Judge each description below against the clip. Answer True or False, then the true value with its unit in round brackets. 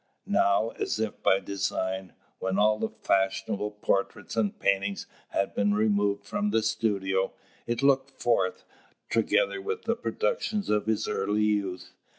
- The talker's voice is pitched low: True (105 Hz)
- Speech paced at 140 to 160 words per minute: True (145 wpm)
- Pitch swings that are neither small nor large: False (2.3 semitones)